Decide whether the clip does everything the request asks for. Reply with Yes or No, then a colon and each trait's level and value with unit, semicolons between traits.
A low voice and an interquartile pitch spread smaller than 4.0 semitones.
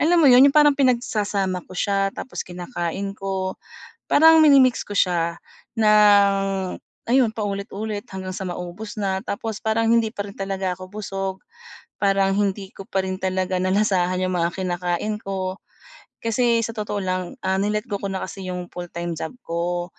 No: high, 195 Hz; narrow, 2.4 semitones